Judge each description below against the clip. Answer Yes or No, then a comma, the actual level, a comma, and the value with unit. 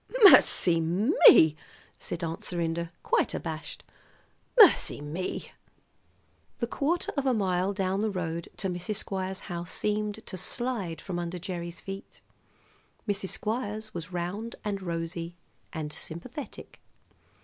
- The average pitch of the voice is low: No, medium, 185 Hz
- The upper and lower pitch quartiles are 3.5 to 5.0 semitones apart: Yes, average, 3.8 semitones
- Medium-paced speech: No, slow, 125 wpm